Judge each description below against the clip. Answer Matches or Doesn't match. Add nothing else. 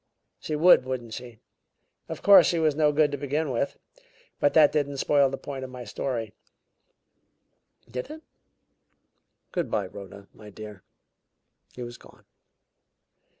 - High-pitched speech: Doesn't match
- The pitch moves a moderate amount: Matches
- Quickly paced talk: Doesn't match